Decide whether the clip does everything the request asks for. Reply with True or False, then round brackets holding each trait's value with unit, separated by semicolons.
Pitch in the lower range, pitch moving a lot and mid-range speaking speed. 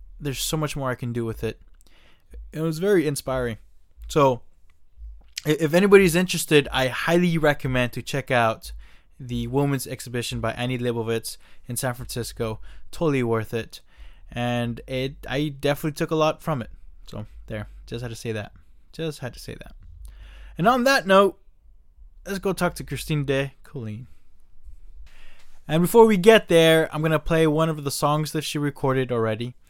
True (125 Hz; 7.4 semitones; 170 wpm)